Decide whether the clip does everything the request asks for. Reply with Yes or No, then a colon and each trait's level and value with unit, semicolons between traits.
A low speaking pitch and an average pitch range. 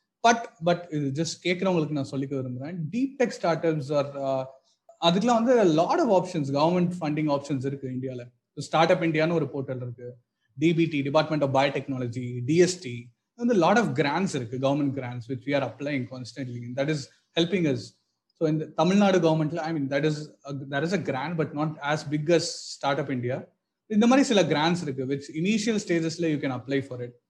No: medium, 150 Hz; average, 3.8 semitones